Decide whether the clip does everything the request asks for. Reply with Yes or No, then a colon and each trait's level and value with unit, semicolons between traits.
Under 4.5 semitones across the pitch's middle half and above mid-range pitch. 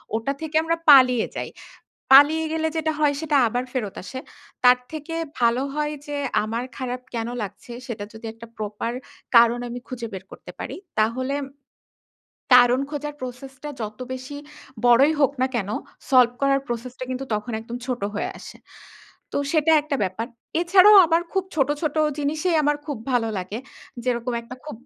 Yes: average, 4.1 semitones; very high, 255 Hz